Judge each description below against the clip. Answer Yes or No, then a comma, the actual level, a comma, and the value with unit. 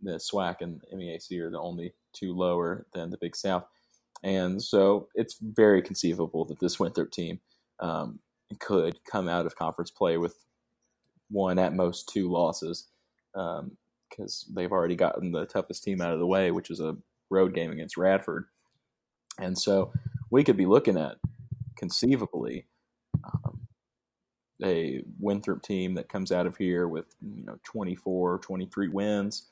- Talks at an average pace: Yes, average, 155 wpm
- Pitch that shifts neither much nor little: No, narrow, 2.1 semitones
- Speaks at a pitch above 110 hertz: No, very low, 95 Hz